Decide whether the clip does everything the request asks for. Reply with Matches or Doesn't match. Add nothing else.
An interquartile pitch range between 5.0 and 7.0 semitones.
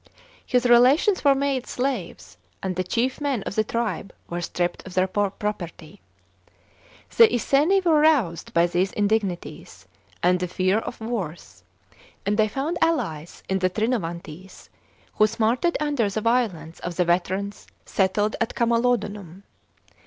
Matches